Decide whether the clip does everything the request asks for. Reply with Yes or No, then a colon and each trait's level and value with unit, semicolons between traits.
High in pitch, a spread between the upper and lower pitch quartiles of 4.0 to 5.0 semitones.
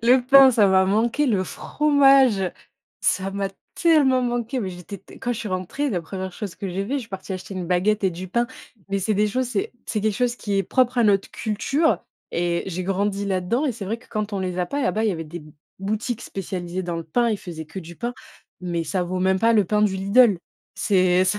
Yes: high, 200 Hz; average, 4.4 semitones